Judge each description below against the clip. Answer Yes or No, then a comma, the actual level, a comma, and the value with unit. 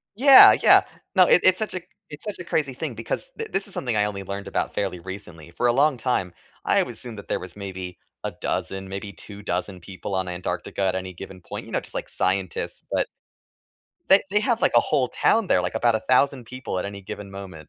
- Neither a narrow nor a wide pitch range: No, wide, 7.0 semitones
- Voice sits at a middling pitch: No, low, 100 Hz